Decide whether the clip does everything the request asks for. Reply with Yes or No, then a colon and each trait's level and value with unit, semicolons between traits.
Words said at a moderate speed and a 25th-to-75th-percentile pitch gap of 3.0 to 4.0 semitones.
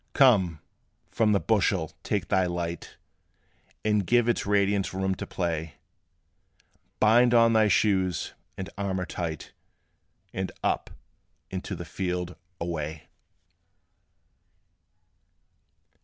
No: slow, 105 wpm; average, 3.4 semitones